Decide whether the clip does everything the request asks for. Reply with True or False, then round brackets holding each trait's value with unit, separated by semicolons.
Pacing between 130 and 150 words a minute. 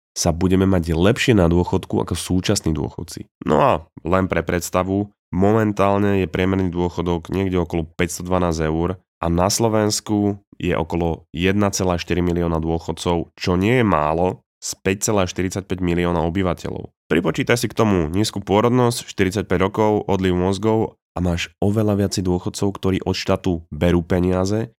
True (140 wpm)